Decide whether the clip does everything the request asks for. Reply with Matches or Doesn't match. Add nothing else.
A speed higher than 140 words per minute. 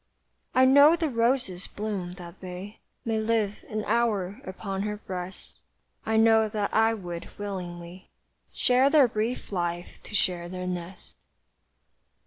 Doesn't match